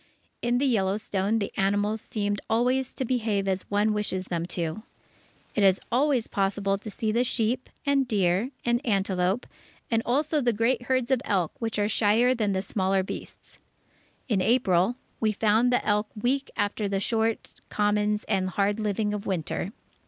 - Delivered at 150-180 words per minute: Yes, average, 165 wpm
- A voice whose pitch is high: Yes, high, 210 Hz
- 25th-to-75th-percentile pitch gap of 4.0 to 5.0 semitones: No, average, 3.3 semitones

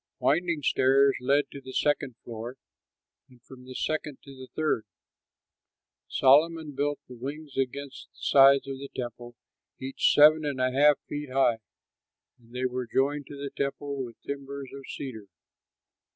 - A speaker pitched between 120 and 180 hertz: Yes, low, 135 Hz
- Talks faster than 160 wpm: No, average, 155 wpm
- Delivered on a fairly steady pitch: Yes, narrow, 2.0 semitones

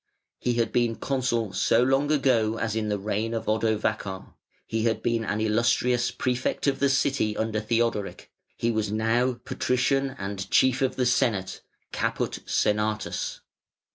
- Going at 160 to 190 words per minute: No, average, 150 wpm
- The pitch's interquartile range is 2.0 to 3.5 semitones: Yes, average, 2.7 semitones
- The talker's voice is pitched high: No, low, 115 Hz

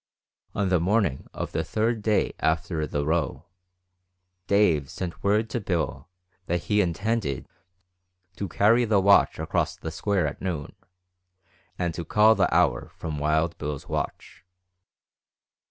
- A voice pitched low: Yes, very low, 90 Hz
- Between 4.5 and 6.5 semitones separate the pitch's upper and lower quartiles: Yes, average, 4.8 semitones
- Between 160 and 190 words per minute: No, average, 140 wpm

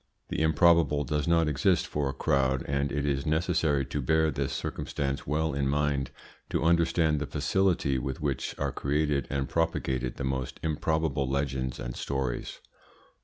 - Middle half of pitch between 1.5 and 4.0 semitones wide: Yes, average, 2.7 semitones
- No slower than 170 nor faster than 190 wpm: No, average, 160 wpm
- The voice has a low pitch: Yes, very low, 70 Hz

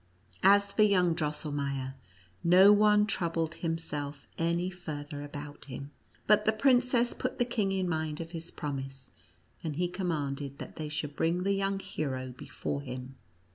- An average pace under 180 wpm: Yes, average, 155 wpm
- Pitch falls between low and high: Yes, medium, 165 Hz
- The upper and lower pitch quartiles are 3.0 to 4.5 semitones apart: No, average, 5.1 semitones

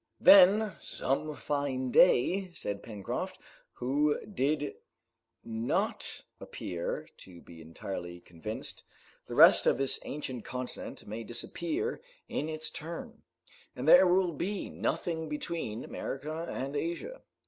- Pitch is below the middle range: No, medium, 145 Hz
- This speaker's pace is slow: Yes, slow, 115 wpm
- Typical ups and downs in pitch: No, wide, 6.9 semitones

